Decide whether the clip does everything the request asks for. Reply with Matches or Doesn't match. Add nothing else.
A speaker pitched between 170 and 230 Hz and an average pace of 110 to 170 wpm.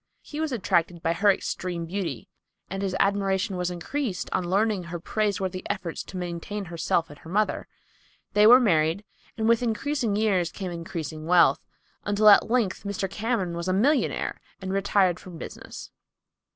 Matches